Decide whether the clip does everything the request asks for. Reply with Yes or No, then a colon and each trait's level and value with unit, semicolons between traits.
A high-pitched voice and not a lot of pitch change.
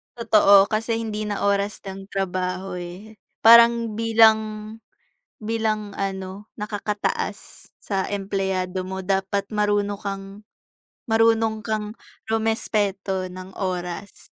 Yes: high, 205 Hz; narrow, 2.2 semitones